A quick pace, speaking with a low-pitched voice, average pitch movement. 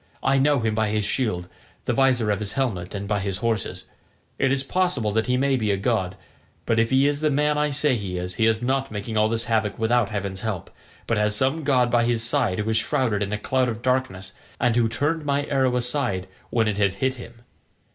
Yes: fast, 235 wpm; low, 115 Hz; average, 4.0 semitones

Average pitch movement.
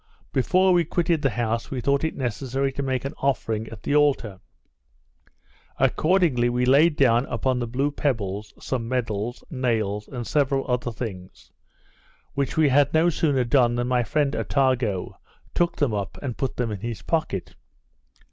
Yes: average, 3.7 semitones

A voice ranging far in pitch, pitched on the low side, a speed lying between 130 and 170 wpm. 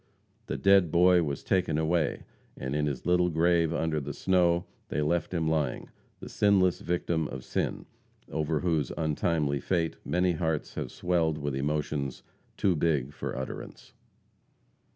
No: average, 3.0 semitones; very low, 80 Hz; average, 150 wpm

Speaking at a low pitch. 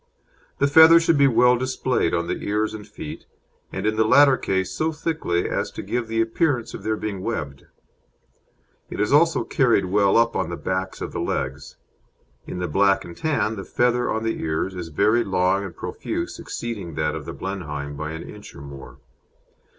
Yes: low, 105 Hz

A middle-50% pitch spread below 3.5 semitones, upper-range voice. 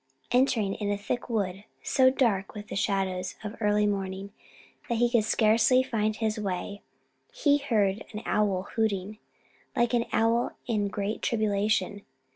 Yes: narrow, 2.5 semitones; high, 210 Hz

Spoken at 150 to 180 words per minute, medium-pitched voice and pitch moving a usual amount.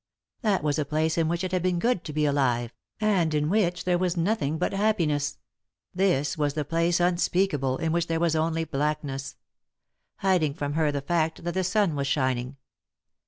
No: average, 190 wpm; medium, 160 Hz; average, 3.6 semitones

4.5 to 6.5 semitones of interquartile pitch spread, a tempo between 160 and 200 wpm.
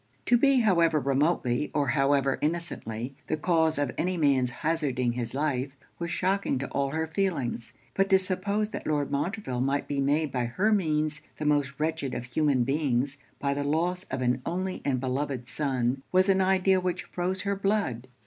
Yes: average, 5.1 semitones; average, 180 wpm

